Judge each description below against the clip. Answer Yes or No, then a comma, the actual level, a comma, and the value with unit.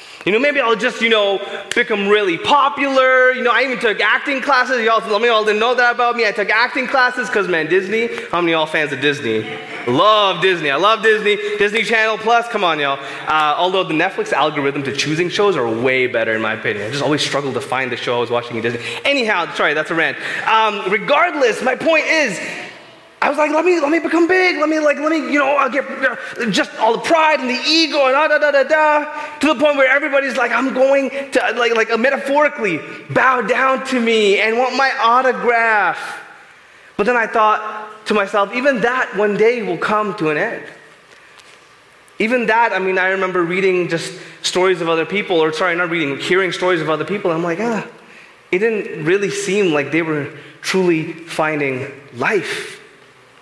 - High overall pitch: Yes, high, 220 Hz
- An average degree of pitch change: No, wide, 7.0 semitones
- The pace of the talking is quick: Yes, fast, 210 wpm